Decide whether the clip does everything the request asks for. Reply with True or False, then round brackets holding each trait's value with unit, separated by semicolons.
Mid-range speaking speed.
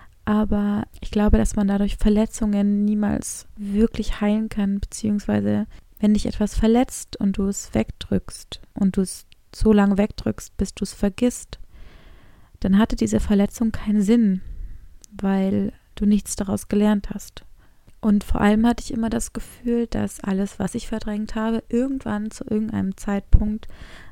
True (150 wpm)